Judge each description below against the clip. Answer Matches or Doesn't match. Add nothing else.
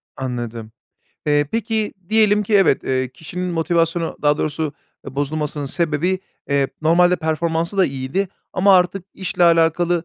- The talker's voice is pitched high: Doesn't match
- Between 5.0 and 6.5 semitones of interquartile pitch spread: Doesn't match